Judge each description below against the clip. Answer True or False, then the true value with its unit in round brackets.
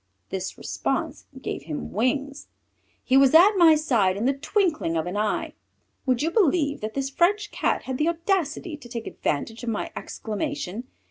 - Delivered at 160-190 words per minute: True (175 wpm)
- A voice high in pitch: True (270 Hz)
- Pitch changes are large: True (6.7 semitones)